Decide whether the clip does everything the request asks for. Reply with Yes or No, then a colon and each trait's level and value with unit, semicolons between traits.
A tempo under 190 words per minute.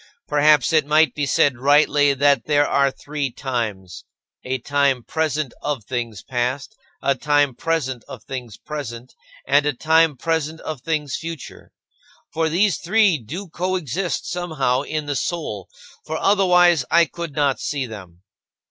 Yes: average, 150 wpm